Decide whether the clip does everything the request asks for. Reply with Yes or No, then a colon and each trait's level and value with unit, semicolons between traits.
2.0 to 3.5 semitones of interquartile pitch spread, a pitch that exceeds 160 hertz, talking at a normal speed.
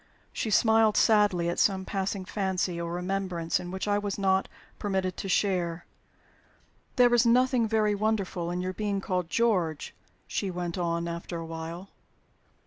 Yes: average, 3.1 semitones; high, 190 Hz; average, 155 wpm